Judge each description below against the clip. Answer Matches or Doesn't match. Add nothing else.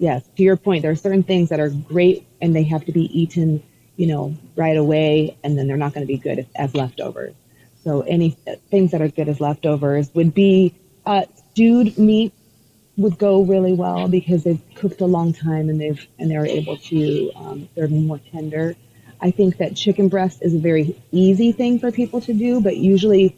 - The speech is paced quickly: Matches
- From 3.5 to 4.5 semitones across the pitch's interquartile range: Matches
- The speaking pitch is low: Doesn't match